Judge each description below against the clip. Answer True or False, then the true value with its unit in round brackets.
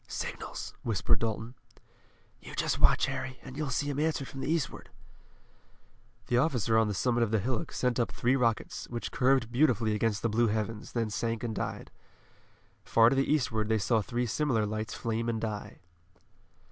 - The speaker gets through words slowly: False (180 wpm)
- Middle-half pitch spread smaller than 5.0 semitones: True (2.8 semitones)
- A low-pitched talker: True (115 Hz)